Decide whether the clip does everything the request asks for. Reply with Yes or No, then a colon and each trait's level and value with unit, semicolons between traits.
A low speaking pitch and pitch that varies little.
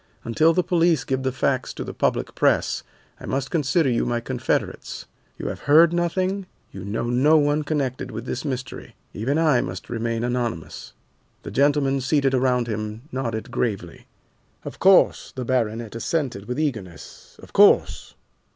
No: low, 130 Hz; average, 4.2 semitones